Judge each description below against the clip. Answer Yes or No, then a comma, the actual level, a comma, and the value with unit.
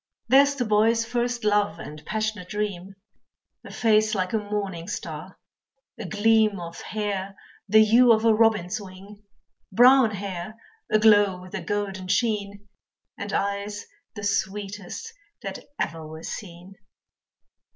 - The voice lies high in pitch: Yes, high, 205 Hz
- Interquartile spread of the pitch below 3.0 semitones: Yes, narrow, 2.4 semitones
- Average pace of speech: No, slow, 130 wpm